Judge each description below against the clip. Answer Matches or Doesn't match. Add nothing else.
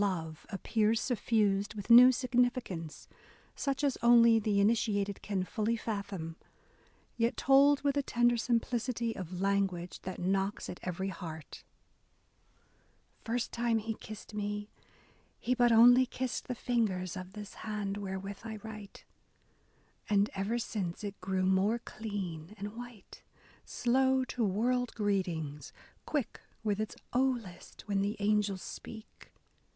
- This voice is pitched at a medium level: Doesn't match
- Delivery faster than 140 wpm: Doesn't match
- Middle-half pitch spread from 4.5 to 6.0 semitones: Doesn't match